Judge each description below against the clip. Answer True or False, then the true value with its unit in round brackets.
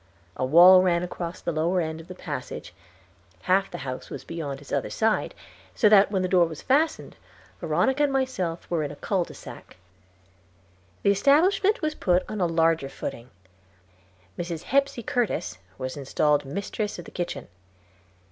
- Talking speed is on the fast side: False (165 wpm)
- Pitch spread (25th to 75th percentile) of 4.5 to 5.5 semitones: True (5.2 semitones)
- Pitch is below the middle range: False (175 Hz)